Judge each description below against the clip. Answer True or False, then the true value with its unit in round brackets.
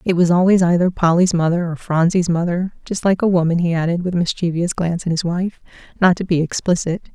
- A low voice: False (175 Hz)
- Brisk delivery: True (220 wpm)